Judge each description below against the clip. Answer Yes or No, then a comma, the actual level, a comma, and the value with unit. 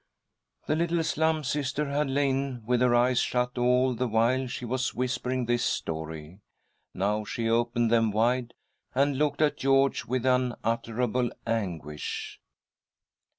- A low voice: Yes, low, 125 Hz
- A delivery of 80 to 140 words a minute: Yes, slow, 135 wpm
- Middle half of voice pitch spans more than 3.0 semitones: No, average, 2.7 semitones